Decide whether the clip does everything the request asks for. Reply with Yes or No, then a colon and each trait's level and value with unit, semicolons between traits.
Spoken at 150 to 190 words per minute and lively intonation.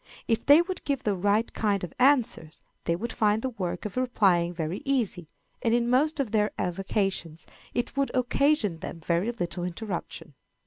Yes: average, 175 wpm; wide, 5.9 semitones